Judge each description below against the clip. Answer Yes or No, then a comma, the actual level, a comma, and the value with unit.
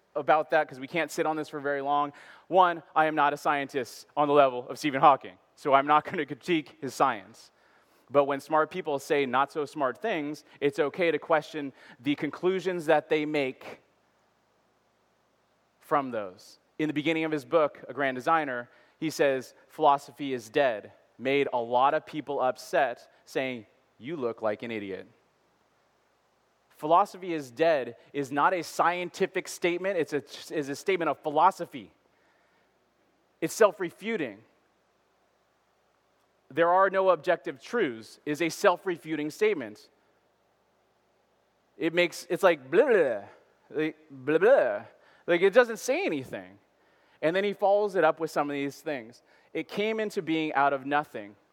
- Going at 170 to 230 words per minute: No, average, 155 wpm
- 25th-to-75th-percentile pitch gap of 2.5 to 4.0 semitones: Yes, average, 3.5 semitones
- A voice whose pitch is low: No, medium, 155 Hz